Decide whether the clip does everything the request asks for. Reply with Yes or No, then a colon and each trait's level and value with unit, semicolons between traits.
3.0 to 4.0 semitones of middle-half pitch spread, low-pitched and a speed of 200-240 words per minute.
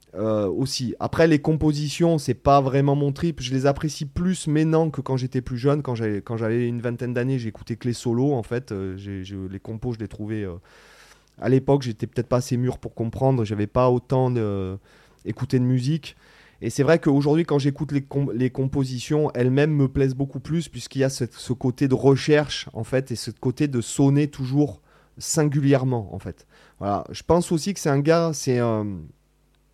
Yes: average, 3.5 semitones; low, 130 Hz; average, 210 wpm